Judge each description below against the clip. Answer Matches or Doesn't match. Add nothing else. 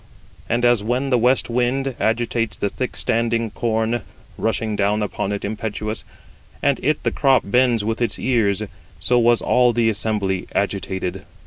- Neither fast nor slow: Matches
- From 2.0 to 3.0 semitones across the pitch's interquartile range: Matches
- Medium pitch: Doesn't match